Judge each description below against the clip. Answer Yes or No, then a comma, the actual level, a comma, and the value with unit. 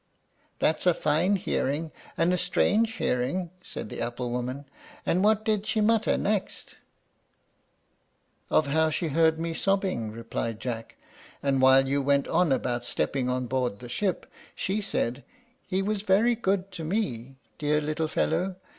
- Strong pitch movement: Yes, wide, 6.9 semitones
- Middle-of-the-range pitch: Yes, medium, 160 Hz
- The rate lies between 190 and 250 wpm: No, average, 155 wpm